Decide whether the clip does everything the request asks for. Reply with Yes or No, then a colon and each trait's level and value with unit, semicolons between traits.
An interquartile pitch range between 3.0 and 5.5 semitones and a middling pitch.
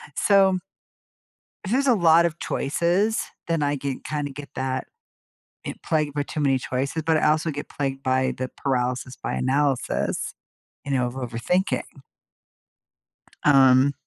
Yes: average, 3.8 semitones; medium, 145 Hz